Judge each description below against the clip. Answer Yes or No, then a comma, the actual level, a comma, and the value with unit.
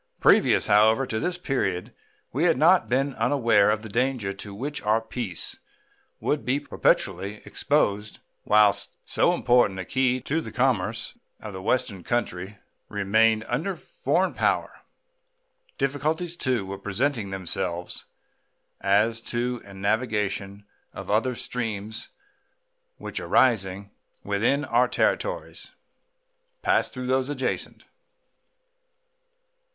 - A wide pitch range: No, average, 4.5 semitones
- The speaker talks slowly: Yes, slow, 115 wpm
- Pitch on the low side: Yes, low, 115 Hz